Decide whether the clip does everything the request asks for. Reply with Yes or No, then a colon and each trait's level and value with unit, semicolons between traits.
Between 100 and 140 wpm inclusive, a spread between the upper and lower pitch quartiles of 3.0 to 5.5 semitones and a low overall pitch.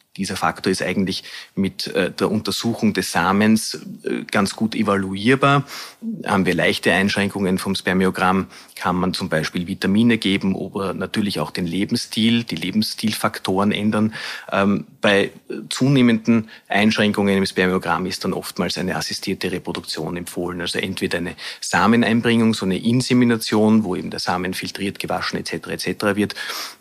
Yes: average, 135 wpm; average, 3.3 semitones; low, 100 Hz